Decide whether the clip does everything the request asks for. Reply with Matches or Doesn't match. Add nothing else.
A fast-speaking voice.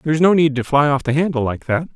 Matches